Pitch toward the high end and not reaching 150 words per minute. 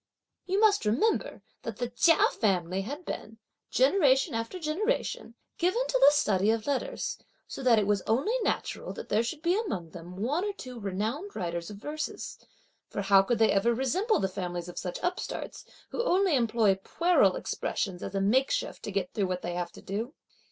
No: high, 230 Hz; average, 185 wpm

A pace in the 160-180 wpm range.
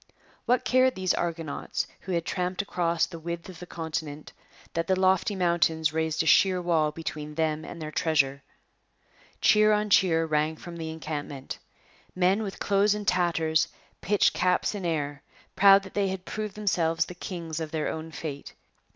Yes: average, 170 wpm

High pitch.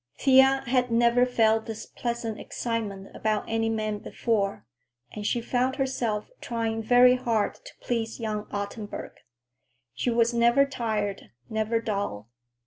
Yes: high, 225 Hz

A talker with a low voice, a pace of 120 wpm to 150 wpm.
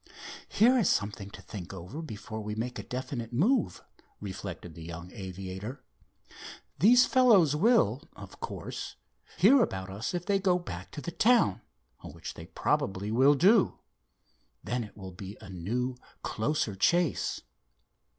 Yes: low, 120 Hz; average, 145 wpm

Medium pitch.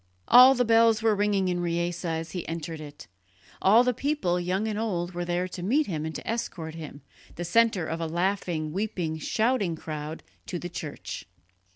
Yes: medium, 175 Hz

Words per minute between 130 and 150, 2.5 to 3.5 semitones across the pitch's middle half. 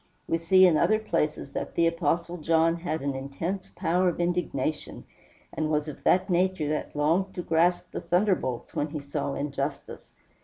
No: average, 175 wpm; average, 3.0 semitones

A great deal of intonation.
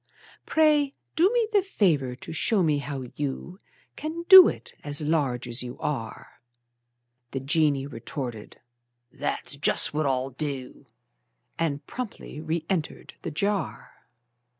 Yes: wide, 6.7 semitones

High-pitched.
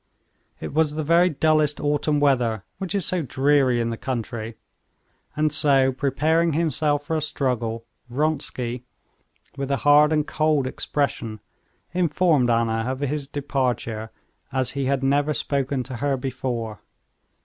No: medium, 140 Hz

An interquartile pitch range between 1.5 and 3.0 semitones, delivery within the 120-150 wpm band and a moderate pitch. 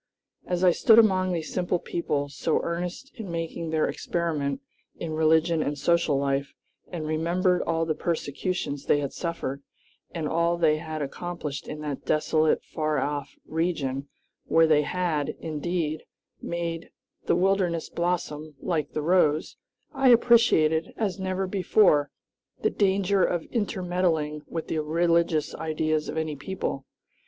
Yes: average, 2.7 semitones; average, 140 wpm; medium, 165 Hz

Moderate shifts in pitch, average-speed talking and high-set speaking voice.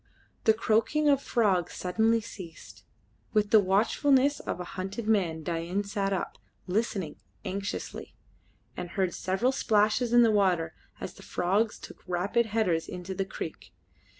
Yes: average, 3.7 semitones; average, 145 wpm; high, 200 Hz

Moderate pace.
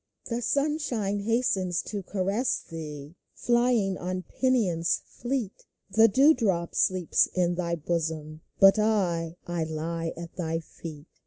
No: slow, 130 wpm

